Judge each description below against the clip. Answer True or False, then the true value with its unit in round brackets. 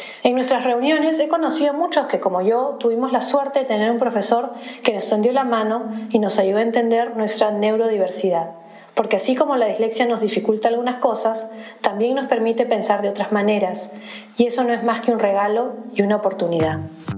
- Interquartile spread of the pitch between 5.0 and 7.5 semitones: False (3.1 semitones)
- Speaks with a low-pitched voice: False (225 Hz)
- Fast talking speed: True (195 wpm)